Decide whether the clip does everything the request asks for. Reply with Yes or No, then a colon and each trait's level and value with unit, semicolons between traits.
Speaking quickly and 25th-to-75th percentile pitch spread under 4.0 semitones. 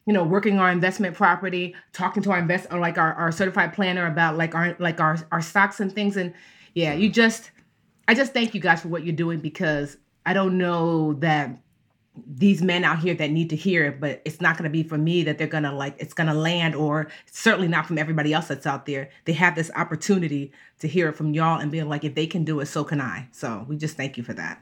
Yes: fast, 250 wpm; average, 2.8 semitones